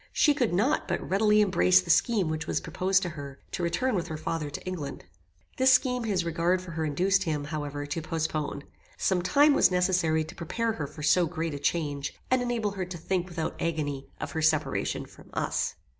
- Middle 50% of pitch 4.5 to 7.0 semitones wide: No, average, 4.0 semitones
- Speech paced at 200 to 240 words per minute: Yes, fast, 205 wpm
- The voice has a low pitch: No, medium, 170 Hz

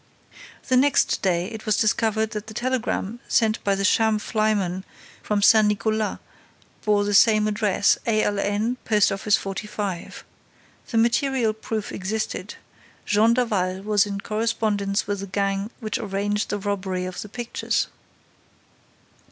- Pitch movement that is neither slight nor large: No, narrow, 1.8 semitones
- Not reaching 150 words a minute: Yes, slow, 135 wpm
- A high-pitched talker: Yes, high, 210 Hz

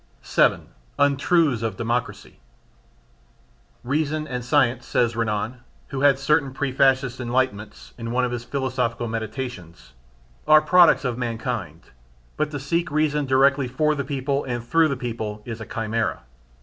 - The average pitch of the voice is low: Yes, low, 130 Hz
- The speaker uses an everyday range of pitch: Yes, average, 3.3 semitones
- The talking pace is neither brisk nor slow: Yes, average, 145 wpm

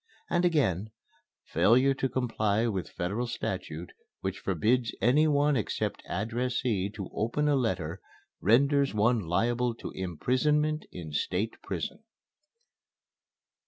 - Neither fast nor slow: No, slow, 115 wpm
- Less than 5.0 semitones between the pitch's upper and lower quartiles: No, wide, 5.6 semitones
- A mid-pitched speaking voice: No, low, 115 Hz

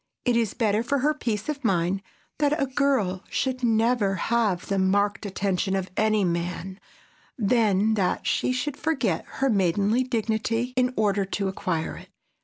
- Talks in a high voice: Yes, high, 215 Hz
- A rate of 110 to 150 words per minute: No, average, 160 wpm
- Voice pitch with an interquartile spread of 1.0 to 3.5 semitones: No, average, 4.5 semitones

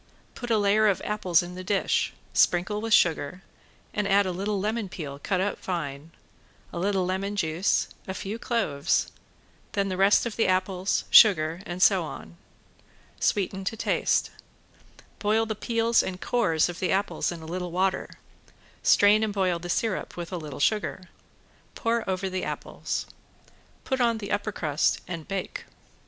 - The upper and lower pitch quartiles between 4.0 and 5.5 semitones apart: No, average, 3.0 semitones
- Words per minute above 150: Yes, average, 165 wpm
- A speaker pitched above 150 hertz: Yes, high, 190 Hz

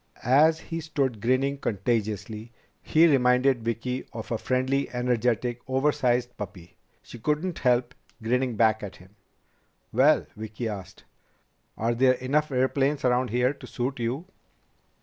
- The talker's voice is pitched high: No, low, 125 Hz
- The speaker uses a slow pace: Yes, slow, 130 wpm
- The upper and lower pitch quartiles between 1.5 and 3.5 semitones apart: Yes, average, 2.8 semitones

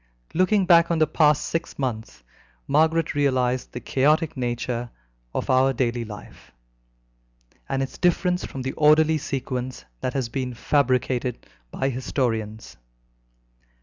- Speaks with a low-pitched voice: Yes, low, 130 Hz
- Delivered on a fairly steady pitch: No, average, 4.0 semitones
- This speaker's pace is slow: Yes, slow, 125 wpm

